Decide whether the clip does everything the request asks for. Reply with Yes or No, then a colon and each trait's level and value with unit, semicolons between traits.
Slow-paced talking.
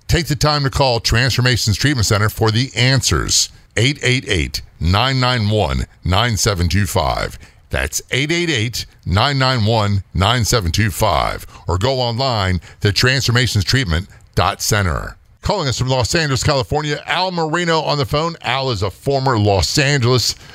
Yes: slow, 115 wpm